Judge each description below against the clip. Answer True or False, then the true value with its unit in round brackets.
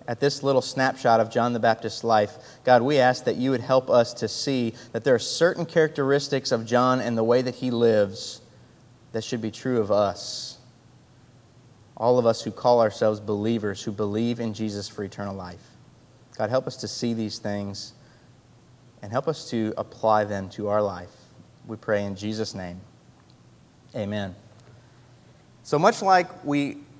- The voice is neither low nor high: False (120 Hz)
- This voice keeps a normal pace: True (175 wpm)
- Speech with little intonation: False (3.0 semitones)